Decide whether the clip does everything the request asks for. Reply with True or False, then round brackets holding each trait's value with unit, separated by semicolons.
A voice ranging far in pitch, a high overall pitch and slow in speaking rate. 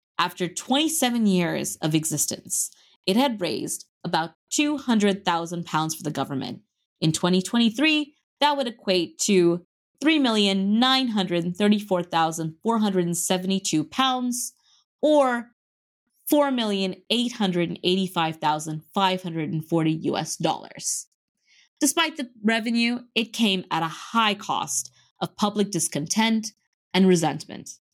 True (6.0 semitones; 195 Hz; 85 wpm)